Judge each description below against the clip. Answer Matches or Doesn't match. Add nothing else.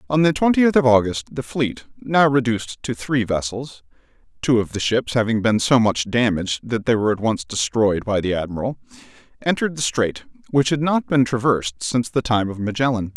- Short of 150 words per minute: Doesn't match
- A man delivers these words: Matches